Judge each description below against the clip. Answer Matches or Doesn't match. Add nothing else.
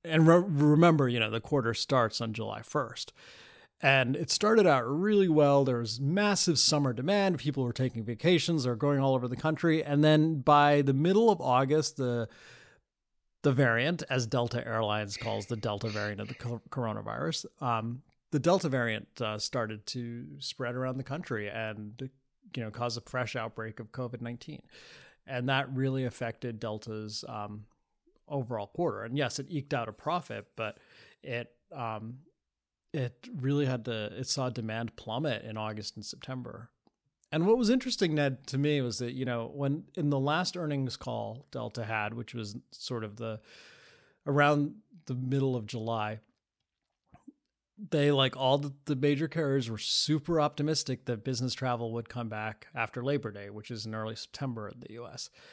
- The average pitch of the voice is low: Matches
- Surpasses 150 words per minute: Matches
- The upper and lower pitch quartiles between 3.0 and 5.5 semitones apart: Matches